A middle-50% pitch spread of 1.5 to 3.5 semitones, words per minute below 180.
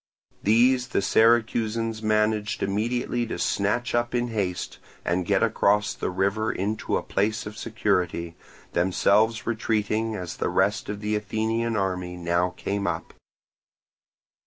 Yes: narrow, 2.4 semitones; slow, 135 wpm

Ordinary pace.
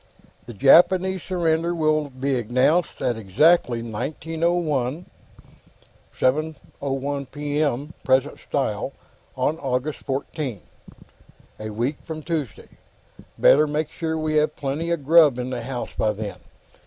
No: slow, 120 wpm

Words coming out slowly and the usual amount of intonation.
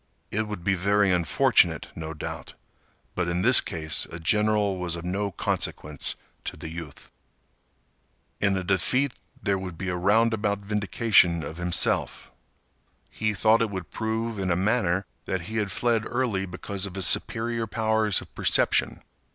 No: average, 160 wpm; average, 3.6 semitones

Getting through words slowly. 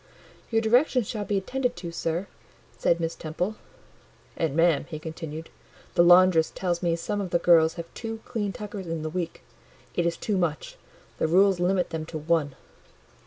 No: average, 175 wpm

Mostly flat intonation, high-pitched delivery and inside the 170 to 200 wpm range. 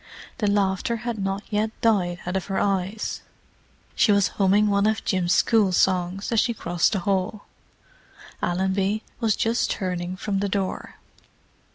No: narrow, 2.2 semitones; high, 195 Hz; average, 155 wpm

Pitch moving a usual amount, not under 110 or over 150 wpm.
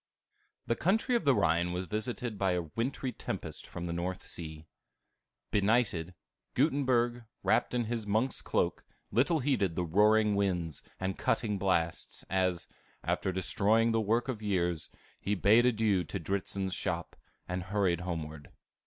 Yes: average, 4.7 semitones; average, 145 wpm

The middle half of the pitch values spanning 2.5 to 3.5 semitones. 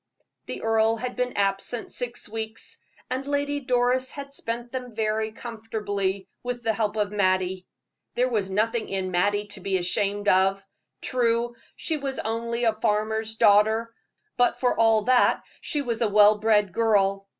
Yes: average, 2.9 semitones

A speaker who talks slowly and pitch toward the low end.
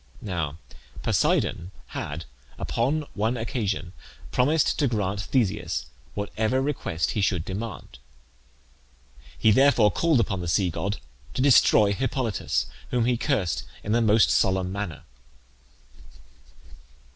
Yes: slow, 115 wpm; low, 105 Hz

